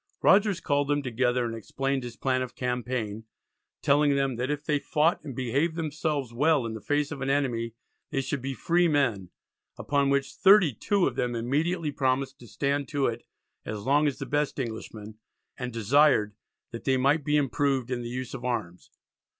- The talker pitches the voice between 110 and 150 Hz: Yes, low, 135 Hz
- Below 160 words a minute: No, average, 180 wpm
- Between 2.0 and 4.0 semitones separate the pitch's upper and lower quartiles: Yes, average, 3.2 semitones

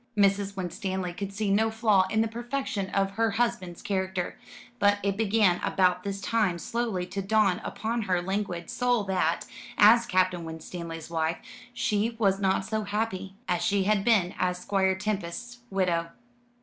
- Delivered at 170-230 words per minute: No, average, 160 wpm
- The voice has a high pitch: Yes, high, 195 Hz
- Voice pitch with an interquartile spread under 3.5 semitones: Yes, average, 3.0 semitones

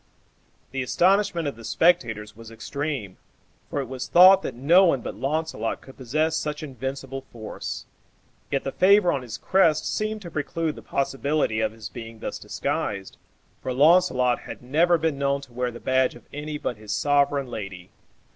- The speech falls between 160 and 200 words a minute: Yes, average, 175 wpm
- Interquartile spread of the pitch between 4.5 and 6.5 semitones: Yes, average, 4.9 semitones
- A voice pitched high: No, low, 135 Hz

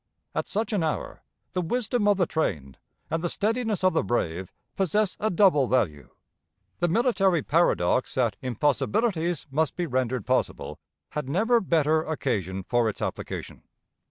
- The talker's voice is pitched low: No, medium, 160 Hz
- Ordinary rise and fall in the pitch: No, wide, 7.7 semitones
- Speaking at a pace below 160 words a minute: Yes, average, 150 wpm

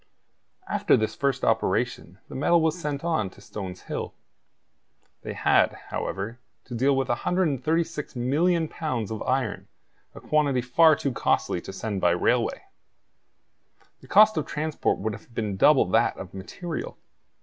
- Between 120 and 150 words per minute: Yes, average, 145 wpm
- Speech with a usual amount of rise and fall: No, wide, 6.3 semitones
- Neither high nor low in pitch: No, low, 130 Hz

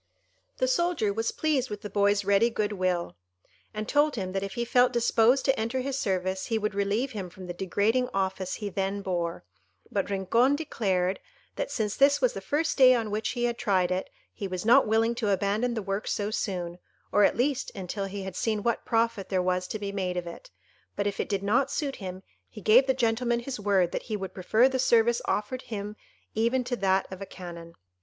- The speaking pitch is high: Yes, high, 210 Hz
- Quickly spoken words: Yes, fast, 220 wpm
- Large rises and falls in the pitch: No, average, 3.9 semitones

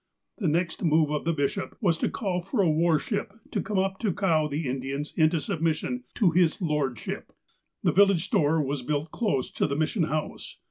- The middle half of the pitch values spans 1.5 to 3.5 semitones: No, average, 4.0 semitones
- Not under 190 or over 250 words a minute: Yes, fast, 205 wpm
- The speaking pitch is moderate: Yes, medium, 160 Hz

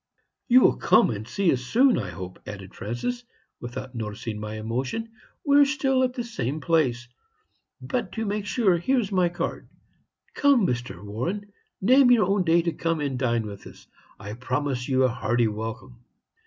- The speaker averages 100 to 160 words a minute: No, average, 180 wpm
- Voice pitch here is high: No, medium, 145 Hz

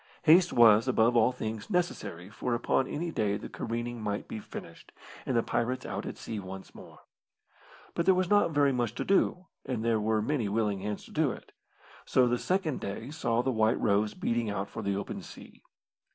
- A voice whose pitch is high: No, low, 115 Hz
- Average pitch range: Yes, average, 4.1 semitones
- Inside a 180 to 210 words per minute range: Yes, average, 200 wpm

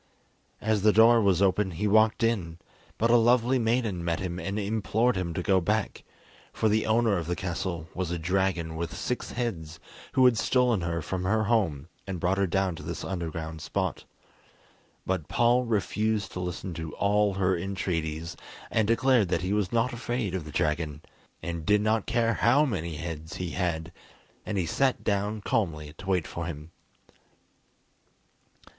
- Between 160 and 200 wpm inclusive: Yes, average, 175 wpm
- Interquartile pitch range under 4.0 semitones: No, average, 4.6 semitones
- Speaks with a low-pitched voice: Yes, very low, 95 Hz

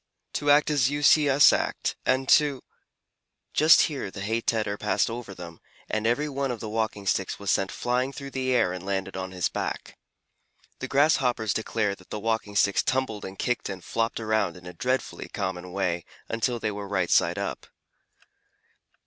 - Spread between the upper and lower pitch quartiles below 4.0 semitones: No, average, 5.0 semitones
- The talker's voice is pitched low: Yes, low, 110 Hz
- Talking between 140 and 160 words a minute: No, average, 190 wpm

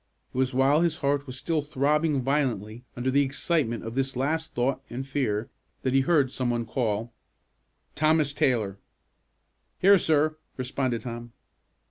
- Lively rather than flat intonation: No, average, 3.4 semitones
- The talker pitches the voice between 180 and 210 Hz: No, low, 135 Hz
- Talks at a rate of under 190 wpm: Yes, average, 150 wpm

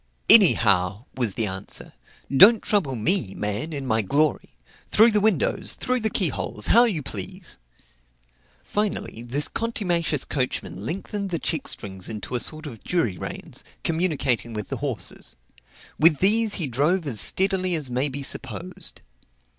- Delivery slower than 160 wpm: Yes, average, 150 wpm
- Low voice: No, medium, 150 Hz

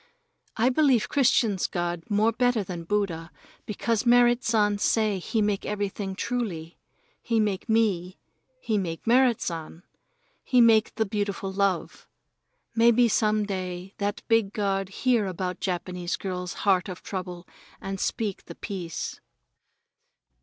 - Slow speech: Yes, slow, 130 wpm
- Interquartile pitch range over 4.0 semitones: No, average, 3.6 semitones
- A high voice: Yes, high, 205 Hz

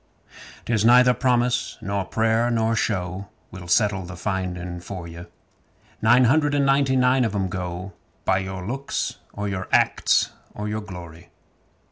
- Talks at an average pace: Yes, average, 150 wpm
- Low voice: Yes, low, 100 Hz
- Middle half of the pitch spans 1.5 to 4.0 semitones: No, average, 4.8 semitones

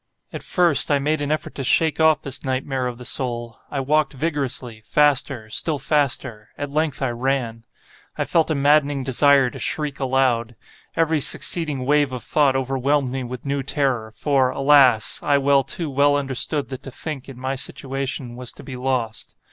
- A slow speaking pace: No, average, 170 wpm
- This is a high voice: No, low, 135 Hz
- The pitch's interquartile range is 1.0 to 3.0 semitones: Yes, narrow, 2.4 semitones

